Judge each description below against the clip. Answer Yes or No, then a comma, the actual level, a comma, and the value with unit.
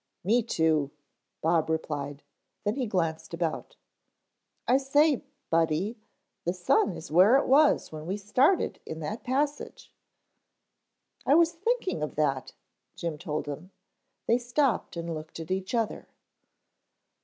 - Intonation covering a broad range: Yes, wide, 8.1 semitones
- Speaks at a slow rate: Yes, slow, 130 wpm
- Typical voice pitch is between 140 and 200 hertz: Yes, medium, 185 Hz